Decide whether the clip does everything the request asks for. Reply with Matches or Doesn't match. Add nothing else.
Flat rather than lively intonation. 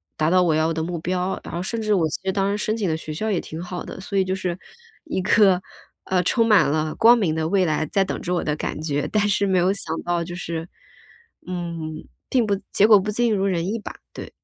Doesn't match